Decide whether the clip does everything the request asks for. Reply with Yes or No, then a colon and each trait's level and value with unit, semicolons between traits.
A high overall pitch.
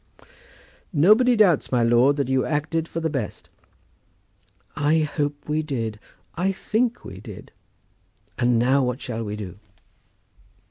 No: medium, 145 Hz